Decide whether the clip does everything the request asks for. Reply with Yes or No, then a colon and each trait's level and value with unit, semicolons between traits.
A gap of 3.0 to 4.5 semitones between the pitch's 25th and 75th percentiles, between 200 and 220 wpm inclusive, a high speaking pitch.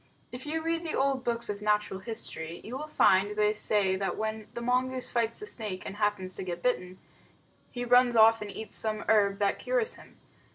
Yes: average, 3.7 semitones; fast, 205 wpm; high, 220 Hz